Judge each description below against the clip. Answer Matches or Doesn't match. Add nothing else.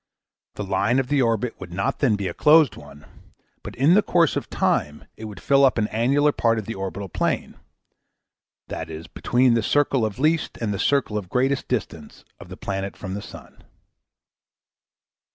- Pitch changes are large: Matches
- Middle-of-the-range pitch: Doesn't match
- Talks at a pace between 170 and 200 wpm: Matches